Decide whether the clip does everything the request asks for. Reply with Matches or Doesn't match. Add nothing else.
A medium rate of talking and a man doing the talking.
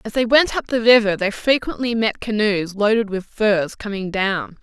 Doesn't match